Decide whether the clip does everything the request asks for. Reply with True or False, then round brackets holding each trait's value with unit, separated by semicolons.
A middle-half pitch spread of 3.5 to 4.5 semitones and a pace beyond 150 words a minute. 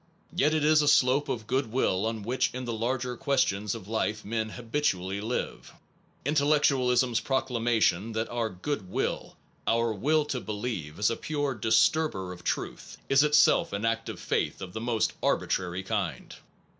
True (4.2 semitones; 170 wpm)